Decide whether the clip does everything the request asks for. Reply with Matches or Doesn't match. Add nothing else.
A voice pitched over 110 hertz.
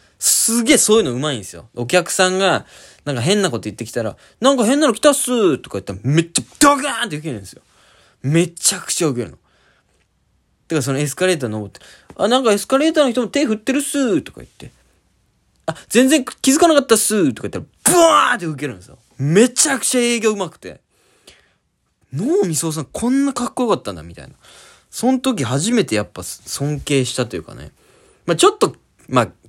Matches